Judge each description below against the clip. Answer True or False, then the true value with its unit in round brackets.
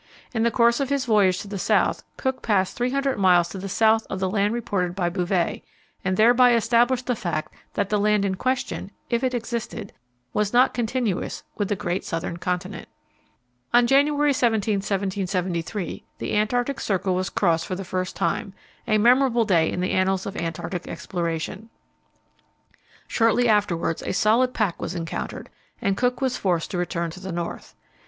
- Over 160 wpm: True (175 wpm)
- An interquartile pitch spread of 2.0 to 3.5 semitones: False (4.4 semitones)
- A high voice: True (200 Hz)